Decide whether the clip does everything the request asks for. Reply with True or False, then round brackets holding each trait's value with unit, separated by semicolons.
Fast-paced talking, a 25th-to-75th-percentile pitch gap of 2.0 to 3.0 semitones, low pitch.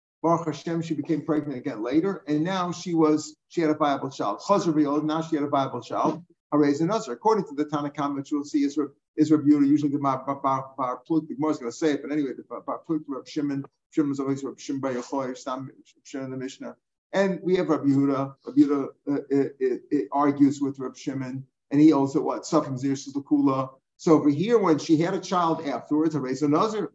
False (225 wpm; 2.4 semitones; 150 Hz)